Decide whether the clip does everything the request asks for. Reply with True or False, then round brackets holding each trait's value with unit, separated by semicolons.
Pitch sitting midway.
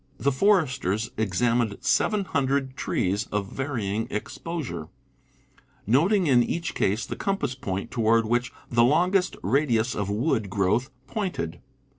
False (120 Hz)